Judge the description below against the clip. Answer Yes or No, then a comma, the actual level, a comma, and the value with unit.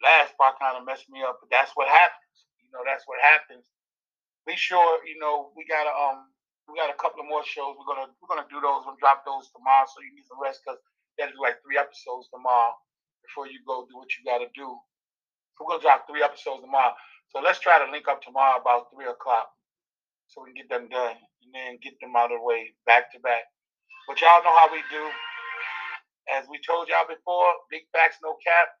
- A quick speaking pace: Yes, fast, 225 wpm